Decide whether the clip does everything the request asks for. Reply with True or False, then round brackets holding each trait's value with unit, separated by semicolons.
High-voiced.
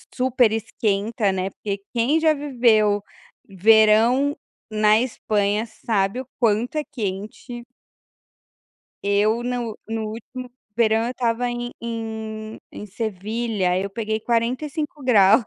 True (225 Hz)